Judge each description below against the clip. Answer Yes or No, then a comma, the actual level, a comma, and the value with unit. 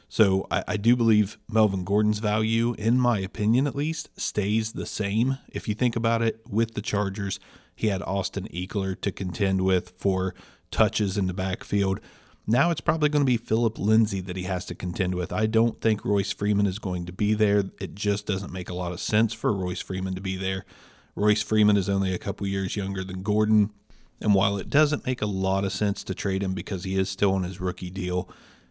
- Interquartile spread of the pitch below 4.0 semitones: Yes, narrow, 2.5 semitones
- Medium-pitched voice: No, low, 100 Hz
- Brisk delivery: Yes, fast, 215 wpm